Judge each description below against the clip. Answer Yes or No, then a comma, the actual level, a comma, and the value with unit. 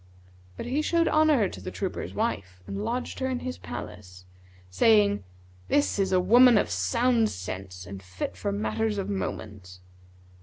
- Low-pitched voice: Yes, low, 115 Hz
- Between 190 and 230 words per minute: No, average, 160 wpm